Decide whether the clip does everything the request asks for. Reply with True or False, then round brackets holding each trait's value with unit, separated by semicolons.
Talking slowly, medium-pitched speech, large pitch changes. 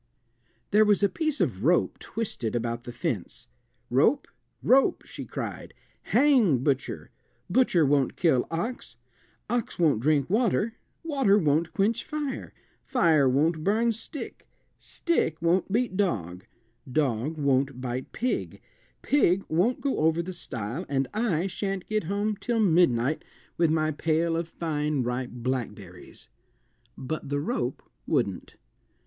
True (130 wpm; 165 Hz; 7.8 semitones)